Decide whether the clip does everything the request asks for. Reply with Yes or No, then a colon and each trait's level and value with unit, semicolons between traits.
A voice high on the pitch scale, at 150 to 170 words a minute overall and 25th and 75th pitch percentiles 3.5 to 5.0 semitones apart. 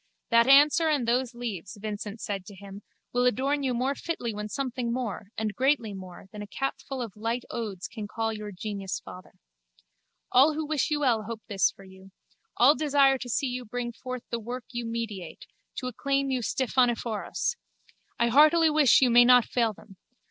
No: high, 240 Hz; average, 185 wpm; average, 4.0 semitones